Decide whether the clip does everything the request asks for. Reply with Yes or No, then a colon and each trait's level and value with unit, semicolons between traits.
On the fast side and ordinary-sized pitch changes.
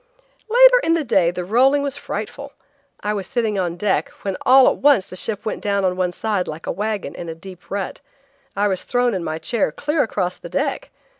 No: fast, 220 wpm; wide, 5.9 semitones